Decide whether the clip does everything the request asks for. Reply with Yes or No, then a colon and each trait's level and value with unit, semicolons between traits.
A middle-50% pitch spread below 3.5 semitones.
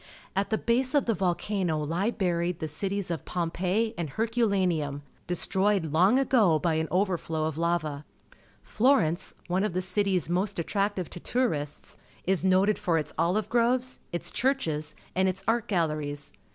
No: average, 4.4 semitones